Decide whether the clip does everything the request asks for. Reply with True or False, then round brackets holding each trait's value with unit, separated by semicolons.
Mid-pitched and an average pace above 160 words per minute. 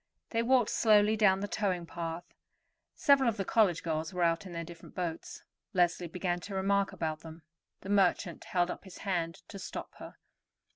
True (180 Hz; 185 wpm)